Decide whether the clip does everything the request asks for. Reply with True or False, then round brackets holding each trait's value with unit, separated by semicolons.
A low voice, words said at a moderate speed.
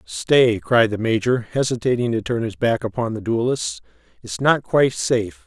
True (120 Hz; 175 wpm)